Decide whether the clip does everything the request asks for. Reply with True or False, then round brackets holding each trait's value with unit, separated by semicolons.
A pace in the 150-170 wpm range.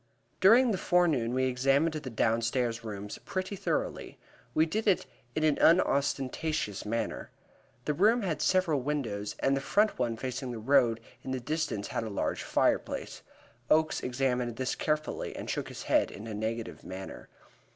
True (160 wpm)